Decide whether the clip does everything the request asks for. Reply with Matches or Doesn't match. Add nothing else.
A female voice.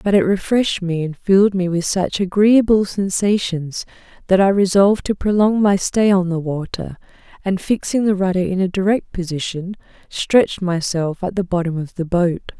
Matches